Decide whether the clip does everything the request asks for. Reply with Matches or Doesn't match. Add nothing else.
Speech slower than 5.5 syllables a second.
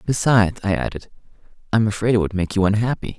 Doesn't match